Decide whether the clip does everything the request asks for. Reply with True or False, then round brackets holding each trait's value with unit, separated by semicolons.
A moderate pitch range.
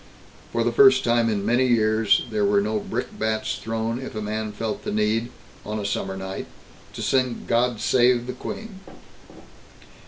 True (3.0 semitones)